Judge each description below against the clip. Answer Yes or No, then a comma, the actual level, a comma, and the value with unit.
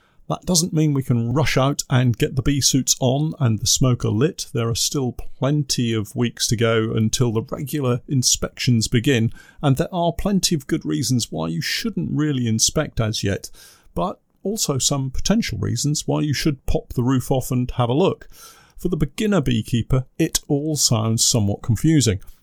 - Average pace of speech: Yes, average, 185 wpm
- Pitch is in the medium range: No, low, 130 Hz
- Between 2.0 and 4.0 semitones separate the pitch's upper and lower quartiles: No, average, 4.6 semitones